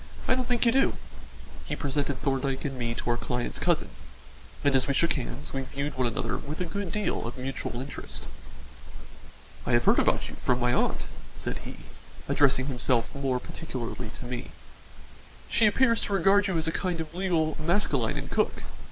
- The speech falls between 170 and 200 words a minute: Yes, average, 185 wpm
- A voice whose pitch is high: No, medium, 140 Hz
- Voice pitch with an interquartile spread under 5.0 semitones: No, wide, 5.4 semitones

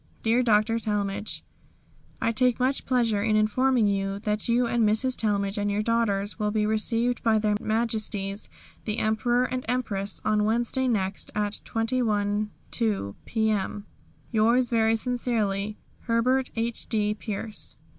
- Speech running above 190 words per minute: No, slow, 135 wpm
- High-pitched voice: Yes, high, 220 Hz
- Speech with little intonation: Yes, narrow, 2.2 semitones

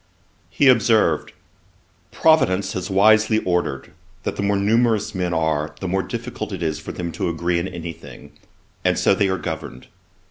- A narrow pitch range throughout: No, average, 4.2 semitones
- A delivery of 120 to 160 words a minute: No, average, 170 wpm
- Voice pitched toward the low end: Yes, very low, 95 Hz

